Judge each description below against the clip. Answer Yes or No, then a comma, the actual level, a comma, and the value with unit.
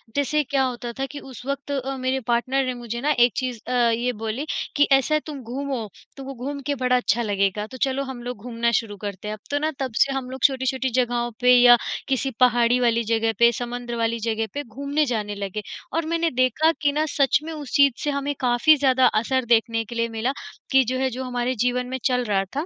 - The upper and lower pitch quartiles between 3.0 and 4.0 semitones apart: No, narrow, 2.5 semitones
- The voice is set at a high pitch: Yes, very high, 250 Hz